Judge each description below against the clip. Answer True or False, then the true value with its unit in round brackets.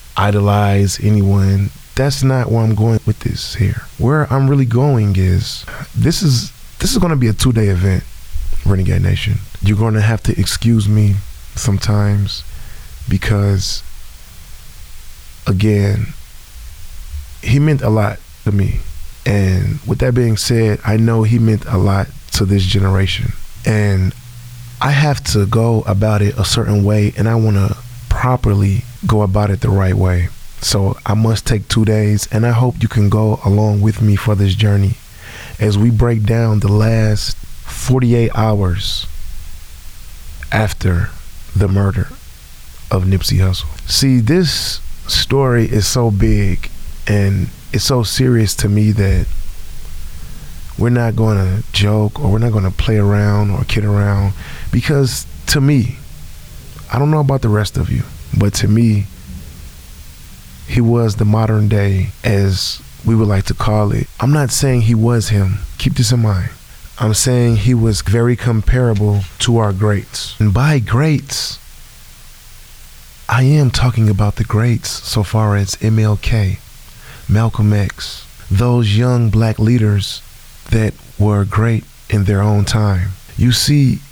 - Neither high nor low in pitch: False (105 Hz)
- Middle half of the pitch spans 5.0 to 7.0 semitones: False (3.3 semitones)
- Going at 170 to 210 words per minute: False (150 wpm)